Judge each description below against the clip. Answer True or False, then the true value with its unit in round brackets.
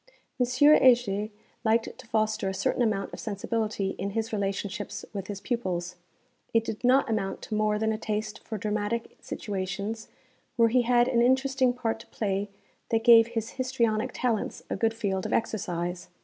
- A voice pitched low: False (220 Hz)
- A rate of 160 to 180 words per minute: True (170 wpm)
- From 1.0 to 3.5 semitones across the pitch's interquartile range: True (2.7 semitones)